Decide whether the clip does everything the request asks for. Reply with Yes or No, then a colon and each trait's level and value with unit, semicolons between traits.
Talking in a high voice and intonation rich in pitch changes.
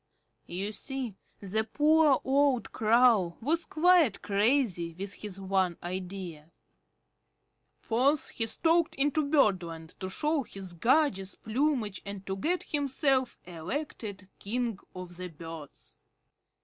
Yes: high, 215 Hz; wide, 7.1 semitones